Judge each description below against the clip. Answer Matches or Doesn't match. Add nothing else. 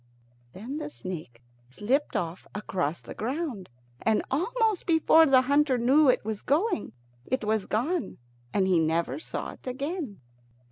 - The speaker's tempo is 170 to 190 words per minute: Doesn't match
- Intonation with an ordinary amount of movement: Doesn't match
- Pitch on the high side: Matches